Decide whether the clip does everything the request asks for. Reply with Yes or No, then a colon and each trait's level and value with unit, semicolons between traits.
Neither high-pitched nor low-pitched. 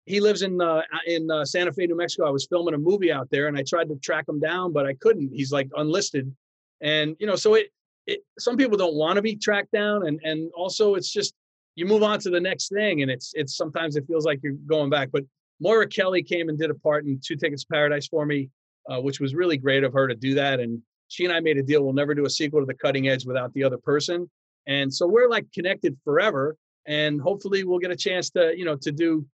Yes: medium, 155 Hz